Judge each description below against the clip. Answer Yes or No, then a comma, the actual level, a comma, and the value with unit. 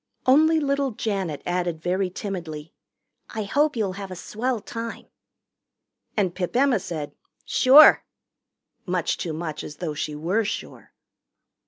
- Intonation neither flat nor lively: No, wide, 5.7 semitones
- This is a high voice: Yes, high, 195 Hz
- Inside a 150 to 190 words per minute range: No, slow, 135 wpm